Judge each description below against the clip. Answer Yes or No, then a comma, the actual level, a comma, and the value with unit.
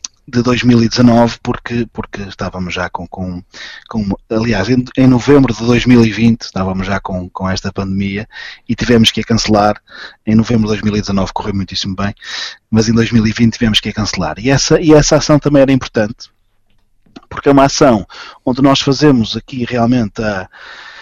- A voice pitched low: Yes, low, 115 Hz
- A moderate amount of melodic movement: Yes, average, 3.7 semitones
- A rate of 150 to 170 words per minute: Yes, average, 165 wpm